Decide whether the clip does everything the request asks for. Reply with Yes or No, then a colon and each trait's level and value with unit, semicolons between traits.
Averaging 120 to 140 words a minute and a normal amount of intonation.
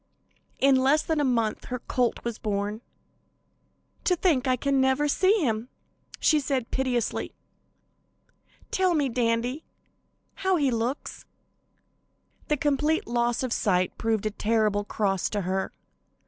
Yes: slow, 135 wpm; average, 4.4 semitones